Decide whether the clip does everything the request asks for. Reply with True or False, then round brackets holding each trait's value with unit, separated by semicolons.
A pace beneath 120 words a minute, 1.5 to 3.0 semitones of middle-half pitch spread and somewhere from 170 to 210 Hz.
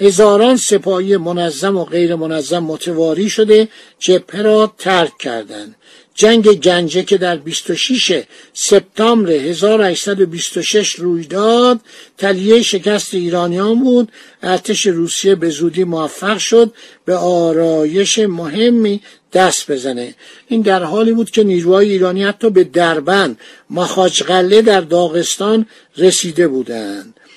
False (110 wpm; 3.6 semitones; 190 Hz)